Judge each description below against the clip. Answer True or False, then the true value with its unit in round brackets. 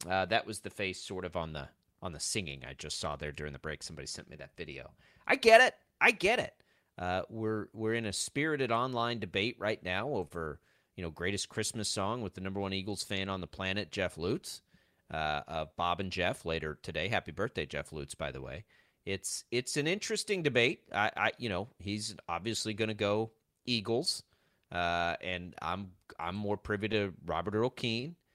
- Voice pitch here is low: True (100 Hz)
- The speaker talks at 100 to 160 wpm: False (200 wpm)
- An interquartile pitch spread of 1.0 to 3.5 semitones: False (4.2 semitones)